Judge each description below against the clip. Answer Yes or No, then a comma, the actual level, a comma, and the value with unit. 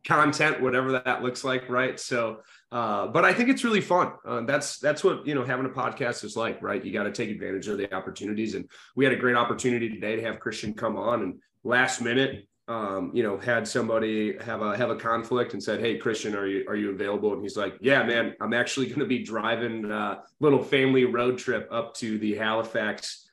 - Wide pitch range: No, average, 2.8 semitones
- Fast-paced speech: Yes, fast, 225 wpm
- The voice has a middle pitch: No, low, 120 Hz